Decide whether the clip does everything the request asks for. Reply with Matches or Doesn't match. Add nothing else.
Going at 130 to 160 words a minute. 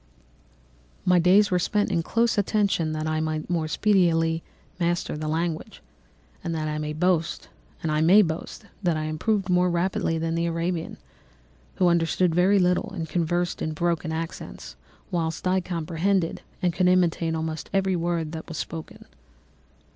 Matches